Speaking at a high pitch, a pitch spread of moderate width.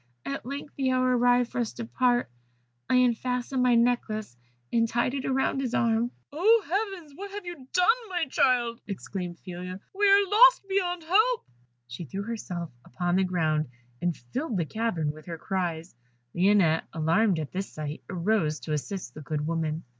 No: high, 230 Hz; wide, 7.7 semitones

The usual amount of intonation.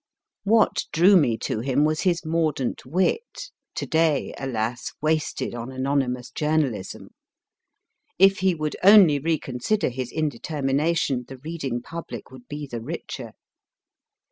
Yes: average, 4.4 semitones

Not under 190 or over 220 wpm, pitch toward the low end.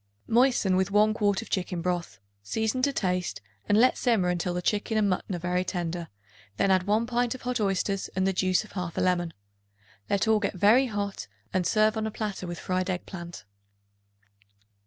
No: average, 195 wpm; high, 195 Hz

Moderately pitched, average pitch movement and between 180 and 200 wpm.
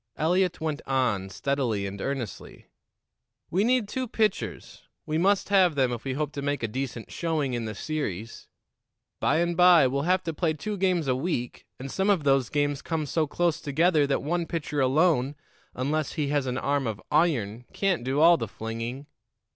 Yes: medium, 145 Hz; average, 4.8 semitones; average, 185 wpm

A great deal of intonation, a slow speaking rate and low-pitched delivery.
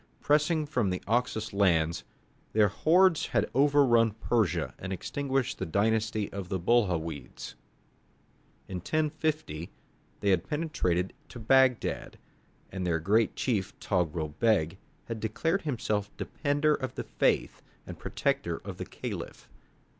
Yes: wide, 6.9 semitones; slow, 130 wpm; low, 110 Hz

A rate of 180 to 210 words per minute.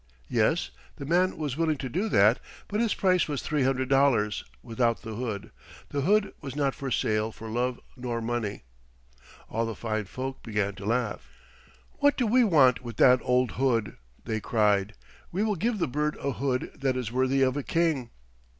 Yes: average, 185 wpm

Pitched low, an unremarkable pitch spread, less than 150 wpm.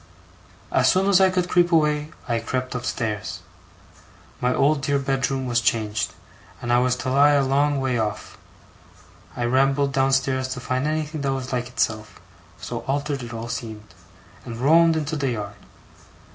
No: low, 130 Hz; average, 3.2 semitones; average, 165 wpm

